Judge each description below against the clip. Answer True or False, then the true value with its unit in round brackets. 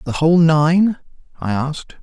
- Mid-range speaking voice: True (160 Hz)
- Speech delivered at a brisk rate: False (150 wpm)